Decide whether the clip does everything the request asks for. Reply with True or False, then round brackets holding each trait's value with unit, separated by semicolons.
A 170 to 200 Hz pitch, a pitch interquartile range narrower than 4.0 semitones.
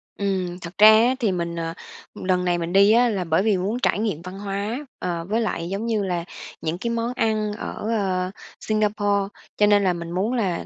True (195 Hz; 3.3 semitones)